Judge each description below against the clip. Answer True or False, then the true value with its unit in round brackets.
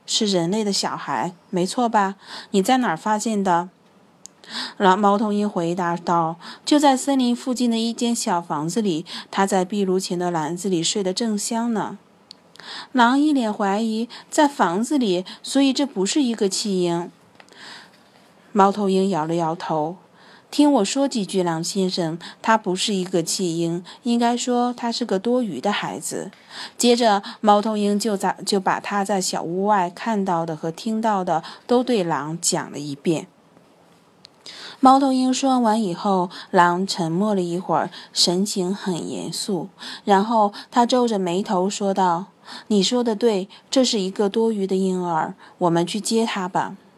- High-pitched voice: True (200 Hz)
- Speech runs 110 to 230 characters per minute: True (225 characters per minute)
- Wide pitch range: False (4.2 semitones)